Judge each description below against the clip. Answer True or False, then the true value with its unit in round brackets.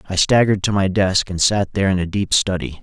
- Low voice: True (95 Hz)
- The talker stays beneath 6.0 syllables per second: False (6.2 syllables/s)